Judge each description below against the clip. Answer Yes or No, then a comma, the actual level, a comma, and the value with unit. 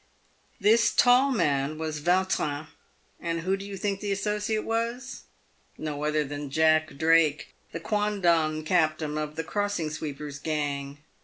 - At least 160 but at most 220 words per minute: No, slow, 135 wpm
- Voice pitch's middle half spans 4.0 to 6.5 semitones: Yes, average, 5.1 semitones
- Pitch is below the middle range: No, medium, 160 Hz